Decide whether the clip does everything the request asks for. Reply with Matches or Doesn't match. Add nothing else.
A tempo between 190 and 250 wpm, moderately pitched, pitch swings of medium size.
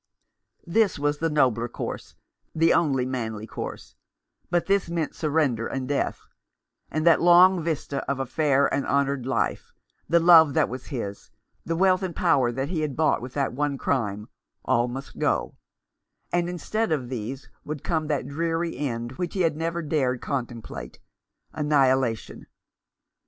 Doesn't match